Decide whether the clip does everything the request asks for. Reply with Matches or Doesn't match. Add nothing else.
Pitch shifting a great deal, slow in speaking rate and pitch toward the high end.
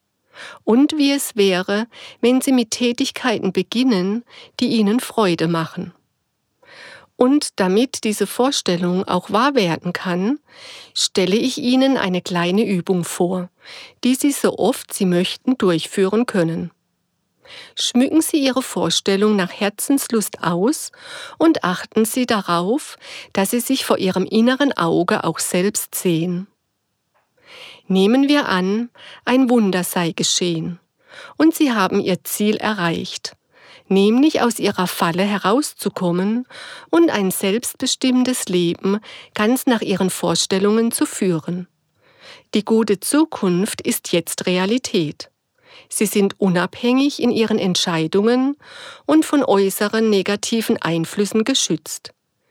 Matches